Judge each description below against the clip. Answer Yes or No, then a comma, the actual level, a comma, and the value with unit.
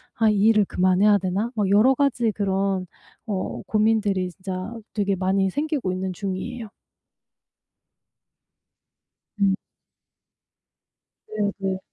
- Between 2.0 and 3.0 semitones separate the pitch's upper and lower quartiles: Yes, narrow, 2.6 semitones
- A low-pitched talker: No, high, 200 Hz